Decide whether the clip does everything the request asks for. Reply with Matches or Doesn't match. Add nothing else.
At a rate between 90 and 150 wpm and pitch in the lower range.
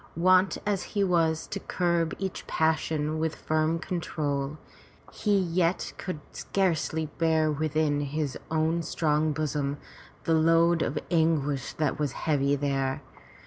Doesn't match